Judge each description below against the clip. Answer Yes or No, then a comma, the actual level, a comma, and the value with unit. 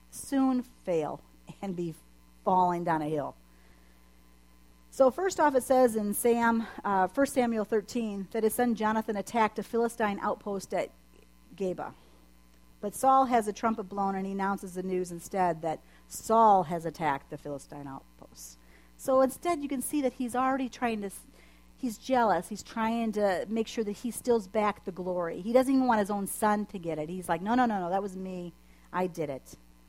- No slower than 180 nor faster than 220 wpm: Yes, average, 185 wpm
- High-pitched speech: Yes, high, 200 Hz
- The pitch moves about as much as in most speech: No, wide, 6.6 semitones